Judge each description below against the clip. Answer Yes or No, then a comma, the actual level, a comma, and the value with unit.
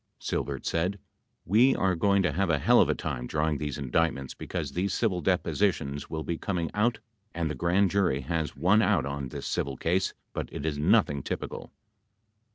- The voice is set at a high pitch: No, very low, 80 Hz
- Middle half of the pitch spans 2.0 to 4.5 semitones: No, average, 4.9 semitones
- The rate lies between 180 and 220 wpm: Yes, average, 190 wpm